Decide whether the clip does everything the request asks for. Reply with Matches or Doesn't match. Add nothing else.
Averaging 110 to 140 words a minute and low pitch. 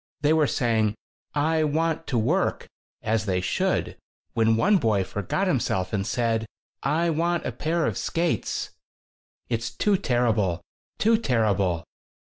Matches